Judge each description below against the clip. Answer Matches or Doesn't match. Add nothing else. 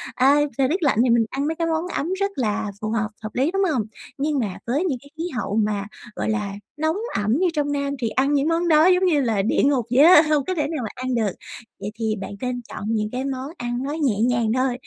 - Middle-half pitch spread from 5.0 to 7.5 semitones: Matches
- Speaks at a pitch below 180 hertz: Doesn't match